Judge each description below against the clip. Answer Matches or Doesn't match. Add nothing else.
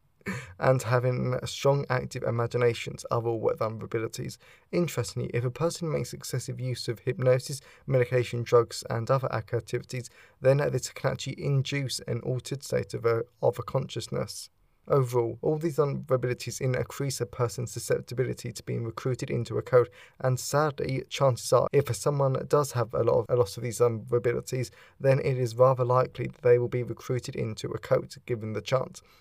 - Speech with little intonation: Matches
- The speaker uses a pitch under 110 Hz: Doesn't match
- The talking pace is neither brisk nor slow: Matches